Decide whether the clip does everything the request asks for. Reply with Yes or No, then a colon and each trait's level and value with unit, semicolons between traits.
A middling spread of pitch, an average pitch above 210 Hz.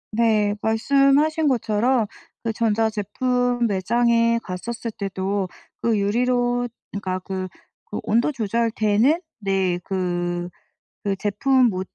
Yes: average, 3.6 semitones; high, 220 Hz